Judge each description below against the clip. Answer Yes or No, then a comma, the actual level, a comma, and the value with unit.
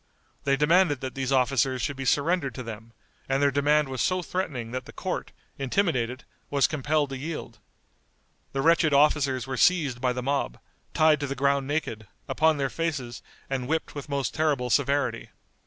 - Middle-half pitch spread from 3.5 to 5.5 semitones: No, average, 2.8 semitones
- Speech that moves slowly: No, average, 175 wpm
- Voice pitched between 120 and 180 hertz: Yes, medium, 140 Hz